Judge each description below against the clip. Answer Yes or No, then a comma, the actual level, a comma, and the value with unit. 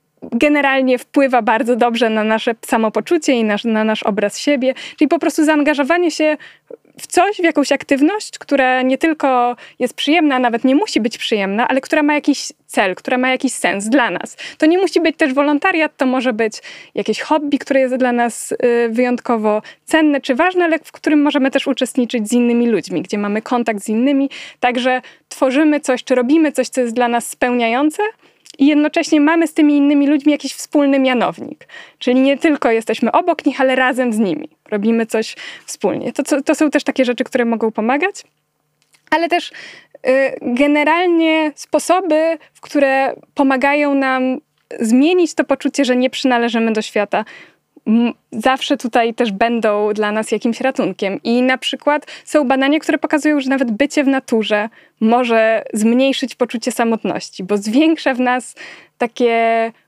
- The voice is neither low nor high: No, very high, 265 Hz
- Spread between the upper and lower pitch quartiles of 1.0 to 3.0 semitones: No, average, 4.2 semitones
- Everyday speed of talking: No, fast, 170 wpm